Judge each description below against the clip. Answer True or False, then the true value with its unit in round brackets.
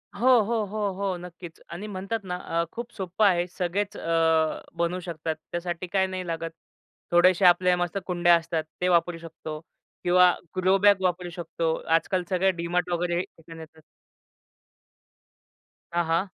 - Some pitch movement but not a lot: False (1.9 semitones)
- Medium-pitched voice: True (180 Hz)